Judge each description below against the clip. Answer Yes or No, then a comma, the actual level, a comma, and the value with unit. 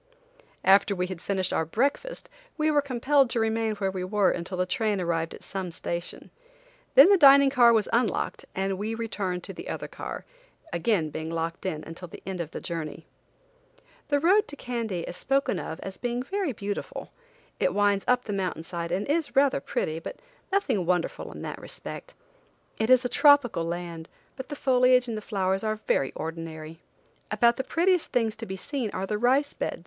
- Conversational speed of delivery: Yes, average, 190 wpm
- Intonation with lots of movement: Yes, wide, 6.2 semitones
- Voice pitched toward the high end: Yes, high, 210 Hz